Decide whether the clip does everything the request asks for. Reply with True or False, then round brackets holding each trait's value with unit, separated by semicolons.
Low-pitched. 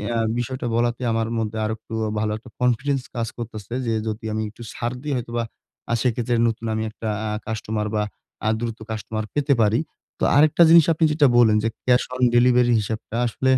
True (115 Hz)